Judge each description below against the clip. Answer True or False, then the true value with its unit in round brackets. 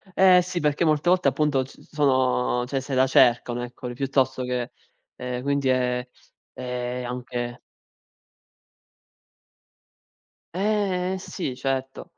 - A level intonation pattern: False (3.2 semitones)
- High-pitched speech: False (130 Hz)